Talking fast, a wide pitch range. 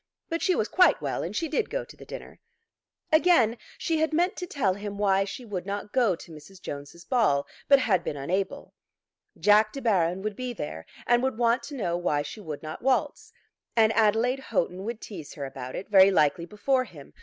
Yes: fast, 210 wpm; wide, 6.4 semitones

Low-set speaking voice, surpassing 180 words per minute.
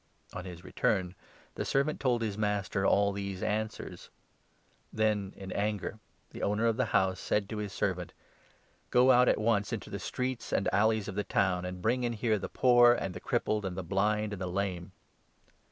Yes: low, 105 Hz; average, 200 wpm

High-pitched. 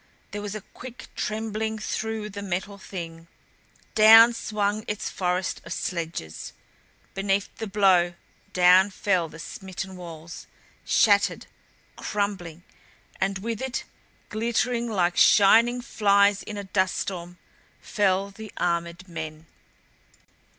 Yes: high, 200 Hz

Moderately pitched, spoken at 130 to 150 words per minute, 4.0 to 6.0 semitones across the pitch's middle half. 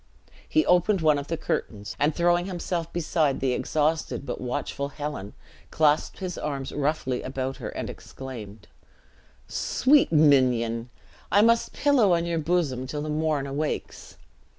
Yes: medium, 150 Hz; average, 145 wpm; average, 4.4 semitones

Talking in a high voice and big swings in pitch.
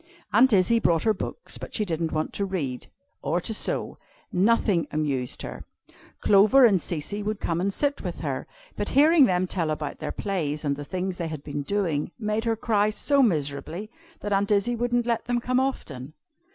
Yes: high, 195 Hz; wide, 6.2 semitones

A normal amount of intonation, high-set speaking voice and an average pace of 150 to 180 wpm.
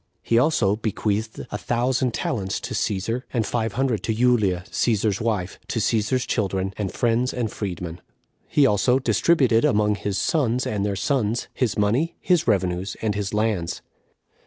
No: average, 3.5 semitones; low, 110 Hz; average, 160 wpm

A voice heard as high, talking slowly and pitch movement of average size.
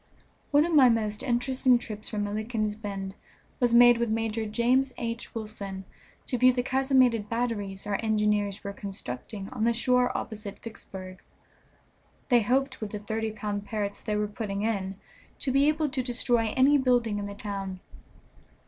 No: high, 220 Hz; average, 165 wpm; average, 3.2 semitones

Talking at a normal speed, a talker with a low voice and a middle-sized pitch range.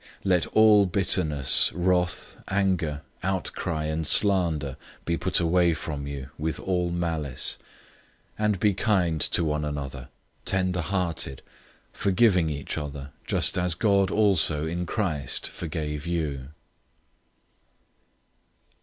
No: slow, 115 wpm; very low, 85 Hz; average, 3.7 semitones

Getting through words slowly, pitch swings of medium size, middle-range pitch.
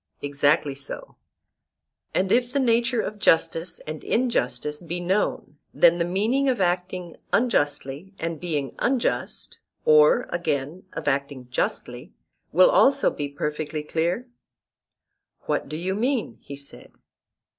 No: slow, 125 wpm; wide, 6.2 semitones; medium, 170 Hz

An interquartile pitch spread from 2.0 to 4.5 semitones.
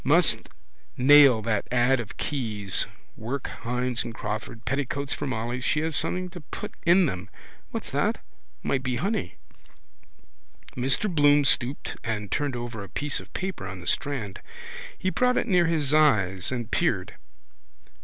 No: average, 4.9 semitones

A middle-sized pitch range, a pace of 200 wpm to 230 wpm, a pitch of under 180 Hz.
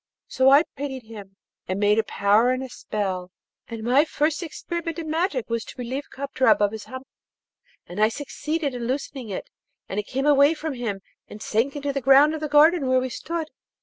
No: average, 4.9 semitones; fast, 205 wpm; very high, 260 Hz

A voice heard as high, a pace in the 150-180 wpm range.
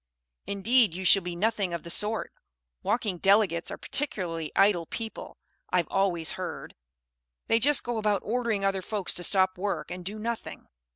Yes: high, 195 Hz; average, 165 wpm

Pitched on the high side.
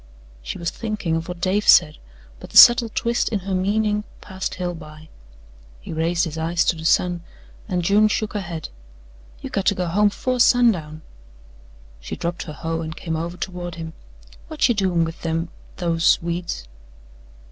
No: medium, 175 Hz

